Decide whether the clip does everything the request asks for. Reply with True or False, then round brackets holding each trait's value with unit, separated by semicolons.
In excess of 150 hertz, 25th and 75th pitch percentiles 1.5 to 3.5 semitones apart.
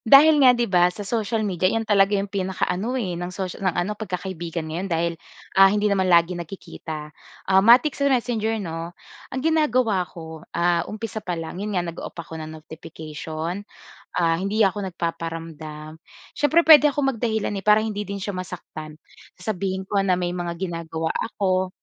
False (190 Hz; 4.1 semitones)